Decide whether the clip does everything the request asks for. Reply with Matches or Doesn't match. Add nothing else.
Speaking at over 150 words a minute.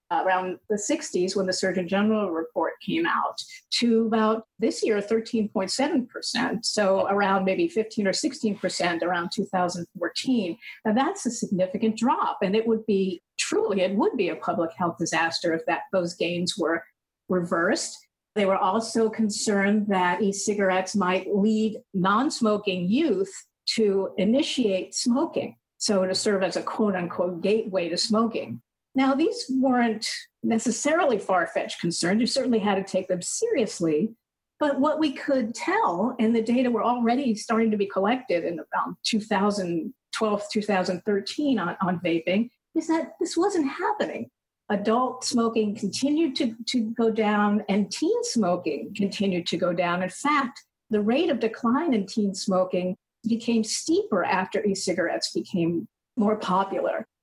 Doesn't match